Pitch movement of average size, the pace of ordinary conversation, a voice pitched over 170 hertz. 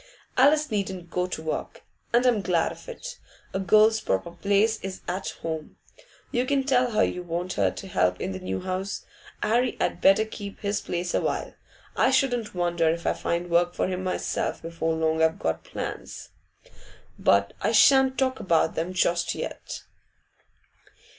Yes: average, 4.6 semitones; average, 170 wpm; medium, 185 Hz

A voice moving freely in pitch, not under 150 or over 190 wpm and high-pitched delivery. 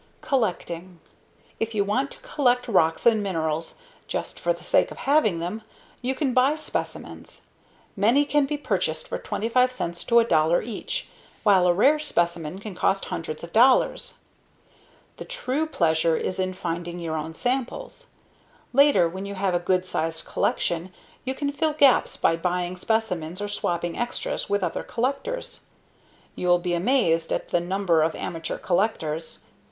Yes: wide, 6.9 semitones; average, 155 wpm; high, 195 Hz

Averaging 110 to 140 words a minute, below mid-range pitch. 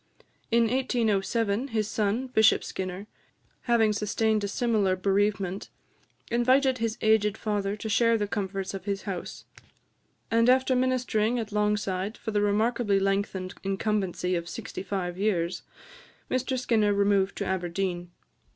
No: slow, 135 wpm; high, 210 Hz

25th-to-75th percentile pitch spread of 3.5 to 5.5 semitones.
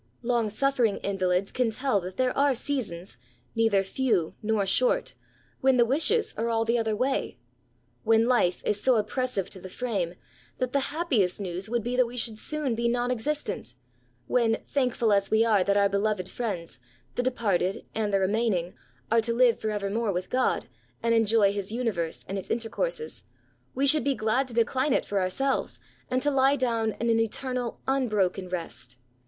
Yes: average, 4.2 semitones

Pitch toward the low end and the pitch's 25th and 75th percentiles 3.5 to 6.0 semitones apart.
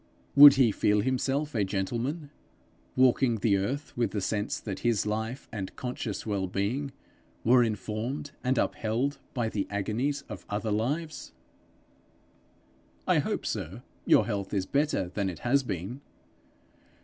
Yes: low, 115 Hz; average, 4.5 semitones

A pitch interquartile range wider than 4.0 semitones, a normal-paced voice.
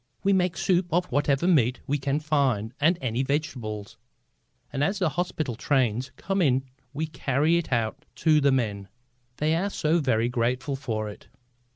Yes: average, 4.5 semitones; average, 170 wpm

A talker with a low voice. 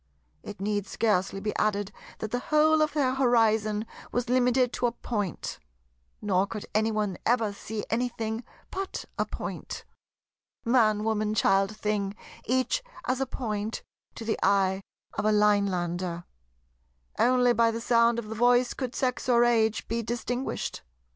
No: high, 220 Hz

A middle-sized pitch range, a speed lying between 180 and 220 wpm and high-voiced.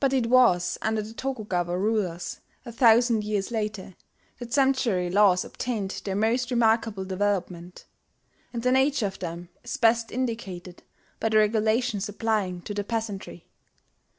No: average, 3.6 semitones; average, 145 wpm; high, 215 Hz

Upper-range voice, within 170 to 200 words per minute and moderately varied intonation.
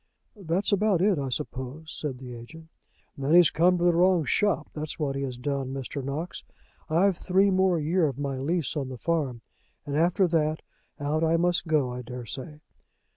No: medium, 155 Hz; average, 190 wpm; average, 4.3 semitones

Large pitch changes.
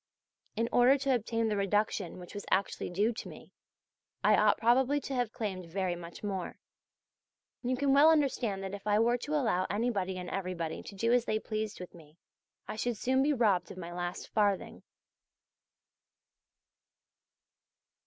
No: average, 4.7 semitones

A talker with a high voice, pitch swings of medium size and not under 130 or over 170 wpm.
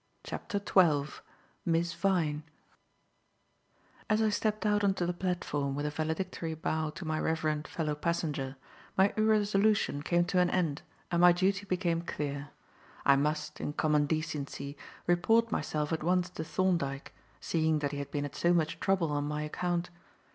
No: medium, 165 Hz; average, 3.5 semitones; average, 160 wpm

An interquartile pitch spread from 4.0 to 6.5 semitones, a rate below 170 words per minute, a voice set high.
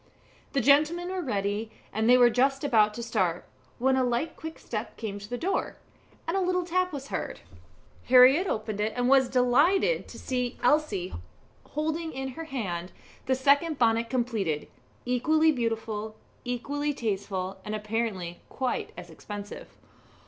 Yes: average, 5.2 semitones; average, 155 wpm; high, 245 Hz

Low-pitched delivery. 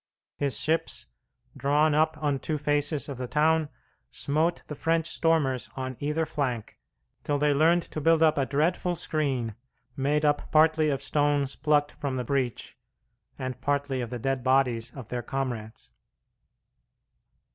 No: medium, 145 Hz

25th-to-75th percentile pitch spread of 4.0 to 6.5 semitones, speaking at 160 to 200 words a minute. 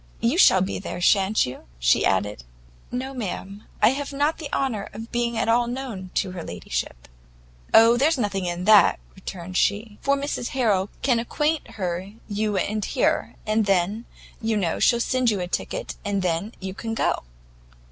Yes: average, 4.3 semitones; average, 175 wpm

